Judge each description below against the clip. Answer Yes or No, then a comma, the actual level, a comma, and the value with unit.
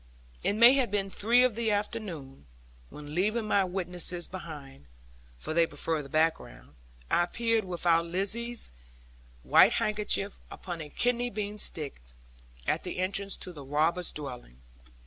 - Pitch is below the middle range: No, medium, 180 Hz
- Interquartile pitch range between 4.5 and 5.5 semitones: Yes, average, 5.2 semitones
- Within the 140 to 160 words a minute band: Yes, average, 145 wpm